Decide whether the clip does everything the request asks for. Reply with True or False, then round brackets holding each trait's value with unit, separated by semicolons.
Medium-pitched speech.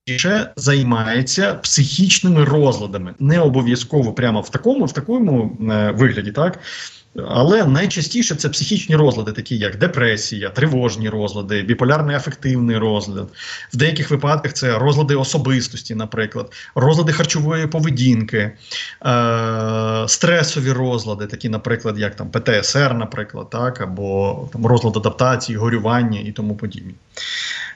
False (125 Hz)